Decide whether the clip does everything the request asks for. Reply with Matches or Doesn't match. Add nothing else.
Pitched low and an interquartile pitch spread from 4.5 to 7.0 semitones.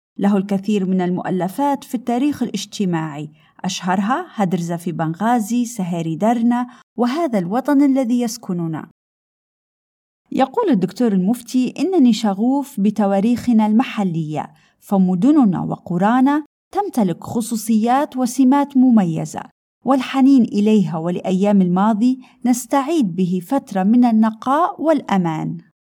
Doesn't match